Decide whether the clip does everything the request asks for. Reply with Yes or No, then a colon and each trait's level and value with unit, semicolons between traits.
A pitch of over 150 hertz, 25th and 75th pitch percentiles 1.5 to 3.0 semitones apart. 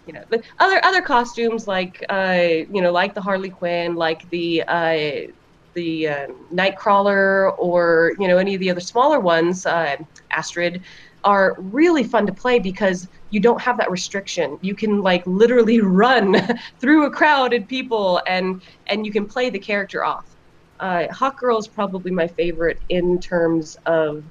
No: high, 190 Hz; average, 4.4 semitones